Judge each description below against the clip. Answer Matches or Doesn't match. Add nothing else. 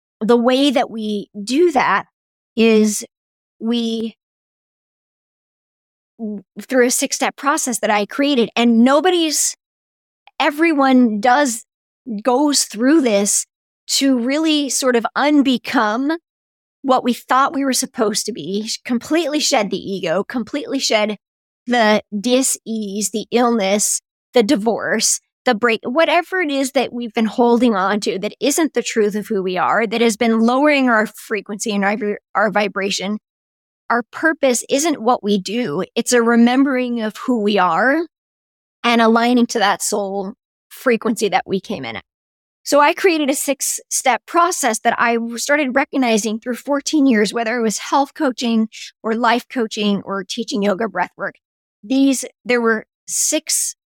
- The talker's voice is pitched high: Matches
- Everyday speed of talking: Matches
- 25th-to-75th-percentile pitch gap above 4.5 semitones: Doesn't match